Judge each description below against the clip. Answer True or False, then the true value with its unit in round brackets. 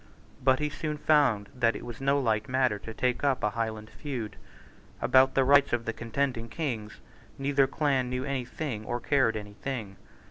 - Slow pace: False (185 wpm)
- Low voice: True (125 Hz)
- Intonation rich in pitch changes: False (3.5 semitones)